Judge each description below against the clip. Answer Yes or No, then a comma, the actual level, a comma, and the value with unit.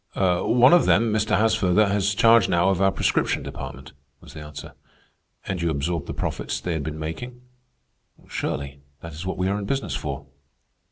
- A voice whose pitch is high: No, very low, 90 Hz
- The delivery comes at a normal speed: Yes, average, 180 wpm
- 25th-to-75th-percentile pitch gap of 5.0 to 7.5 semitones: Yes, wide, 5.6 semitones